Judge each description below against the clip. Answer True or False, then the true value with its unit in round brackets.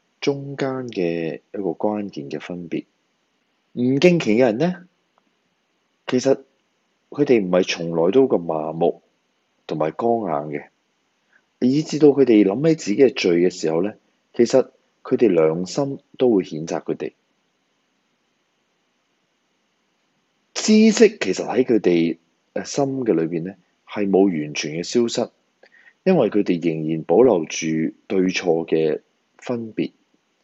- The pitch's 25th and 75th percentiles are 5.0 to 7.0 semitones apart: False (8.6 semitones)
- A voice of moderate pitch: False (105 Hz)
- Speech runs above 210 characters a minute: False (185 characters per minute)